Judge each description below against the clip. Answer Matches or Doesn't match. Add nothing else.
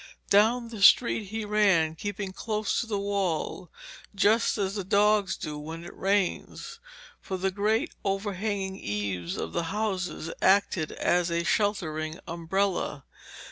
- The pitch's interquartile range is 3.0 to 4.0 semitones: Matches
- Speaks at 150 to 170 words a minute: Doesn't match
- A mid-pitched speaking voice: Doesn't match